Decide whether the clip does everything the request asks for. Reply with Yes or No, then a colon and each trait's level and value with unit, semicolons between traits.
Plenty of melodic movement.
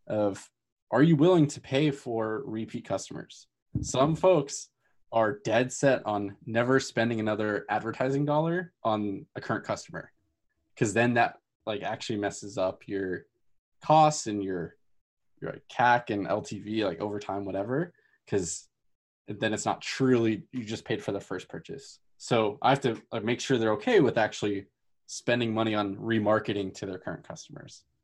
No: average, 4.5 semitones